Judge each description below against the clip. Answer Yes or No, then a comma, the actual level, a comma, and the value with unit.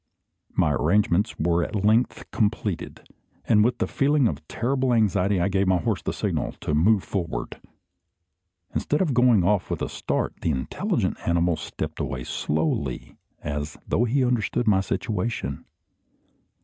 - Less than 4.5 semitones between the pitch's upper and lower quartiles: No, wide, 5.4 semitones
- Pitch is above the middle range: No, low, 100 Hz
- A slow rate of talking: No, average, 150 wpm